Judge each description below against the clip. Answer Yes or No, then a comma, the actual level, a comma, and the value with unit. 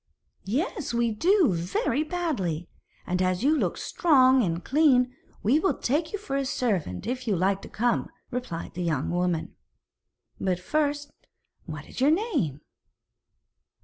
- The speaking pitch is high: Yes, high, 245 Hz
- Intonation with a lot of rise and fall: Yes, wide, 8.5 semitones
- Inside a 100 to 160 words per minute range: Yes, average, 145 wpm